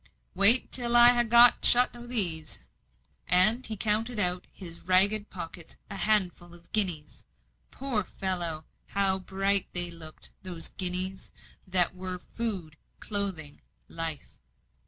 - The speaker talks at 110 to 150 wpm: Yes, slow, 135 wpm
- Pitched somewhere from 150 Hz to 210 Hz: Yes, high, 190 Hz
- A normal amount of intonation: Yes, average, 3.7 semitones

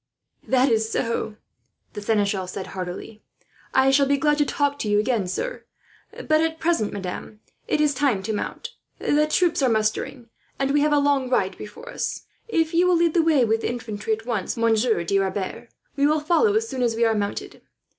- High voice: Yes, very high, 250 Hz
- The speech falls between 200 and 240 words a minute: Yes, fast, 205 wpm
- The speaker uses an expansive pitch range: Yes, wide, 5.9 semitones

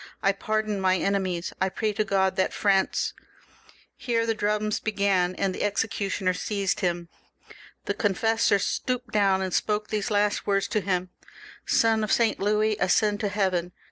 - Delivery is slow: No, average, 165 wpm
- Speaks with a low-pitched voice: No, high, 200 Hz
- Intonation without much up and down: Yes, narrow, 2.1 semitones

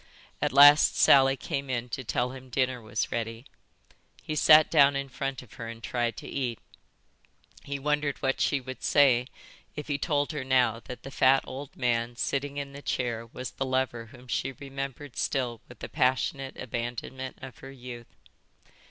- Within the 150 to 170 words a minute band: No, average, 180 wpm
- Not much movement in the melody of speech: Yes, narrow, 2.3 semitones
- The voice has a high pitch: No, low, 130 Hz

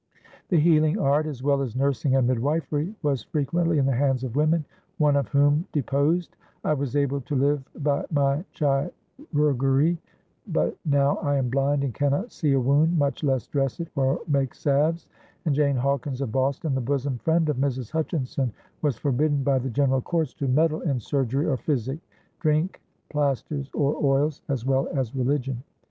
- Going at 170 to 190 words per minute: Yes, average, 175 wpm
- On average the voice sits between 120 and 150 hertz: Yes, medium, 140 Hz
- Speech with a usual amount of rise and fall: No, narrow, 2.1 semitones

